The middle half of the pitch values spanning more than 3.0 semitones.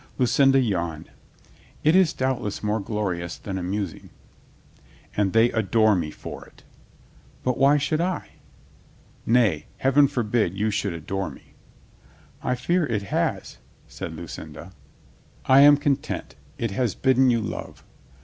Yes: wide, 5.4 semitones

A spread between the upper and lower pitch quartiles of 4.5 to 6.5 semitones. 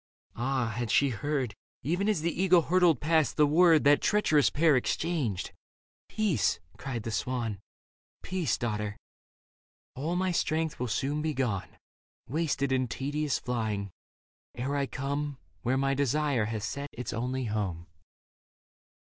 Yes: average, 4.8 semitones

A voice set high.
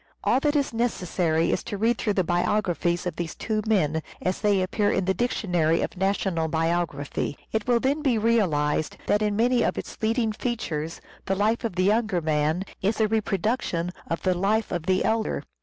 Yes: high, 195 Hz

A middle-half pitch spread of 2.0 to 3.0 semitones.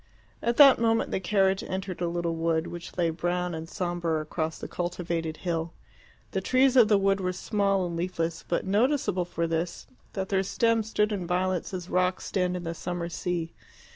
Yes: narrow, 2.6 semitones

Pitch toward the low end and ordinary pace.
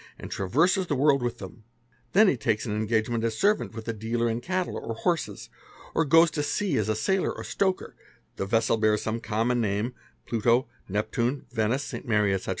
Yes: low, 115 Hz; average, 195 wpm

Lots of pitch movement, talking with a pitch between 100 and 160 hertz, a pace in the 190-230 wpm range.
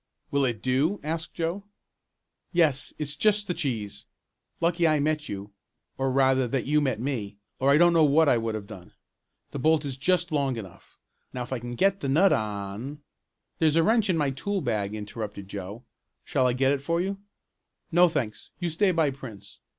Yes: wide, 5.8 semitones; medium, 140 Hz; average, 195 wpm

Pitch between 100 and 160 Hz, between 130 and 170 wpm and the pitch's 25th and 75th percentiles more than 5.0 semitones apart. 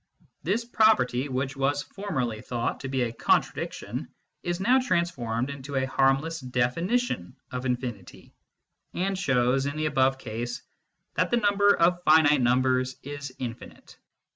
Yes: low, 135 Hz; average, 140 wpm; wide, 5.4 semitones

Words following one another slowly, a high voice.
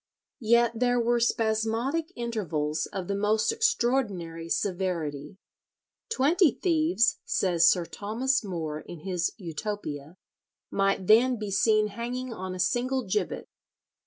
Yes: slow, 120 wpm; high, 215 Hz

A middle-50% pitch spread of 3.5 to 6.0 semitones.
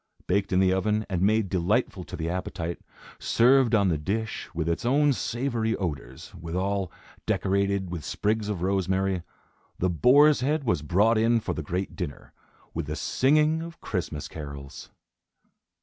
Yes: average, 4.8 semitones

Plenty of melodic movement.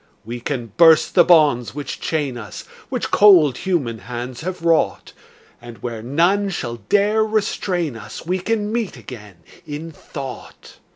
Yes: wide, 7.3 semitones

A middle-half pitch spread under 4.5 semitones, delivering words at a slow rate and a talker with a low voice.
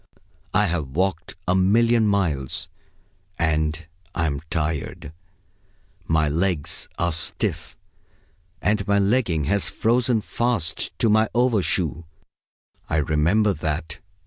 No: average, 5.0 semitones; slow, 105 wpm; very low, 85 Hz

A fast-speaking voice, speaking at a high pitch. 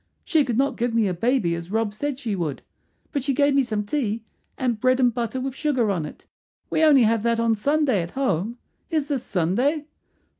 Yes: fast, 215 wpm; high, 240 Hz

